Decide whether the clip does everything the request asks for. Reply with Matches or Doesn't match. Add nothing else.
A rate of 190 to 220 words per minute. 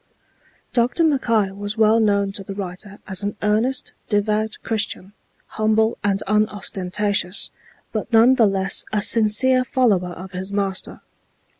Doesn't match